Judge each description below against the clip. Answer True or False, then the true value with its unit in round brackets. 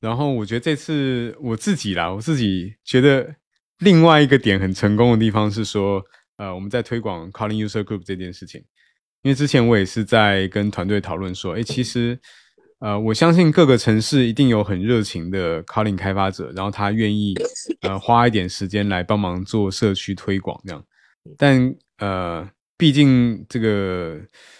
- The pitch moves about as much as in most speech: True (4.3 semitones)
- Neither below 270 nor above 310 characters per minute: True (300 characters per minute)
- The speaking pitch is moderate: False (110 Hz)